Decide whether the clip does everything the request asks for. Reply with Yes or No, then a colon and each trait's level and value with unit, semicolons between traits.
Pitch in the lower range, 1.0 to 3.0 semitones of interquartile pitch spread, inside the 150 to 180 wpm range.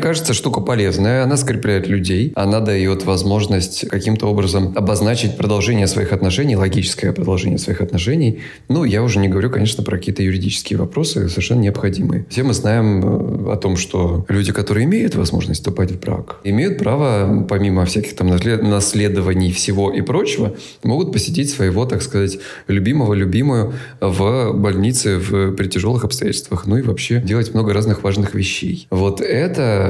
Yes: low, 100 Hz; narrow, 2.5 semitones; average, 155 wpm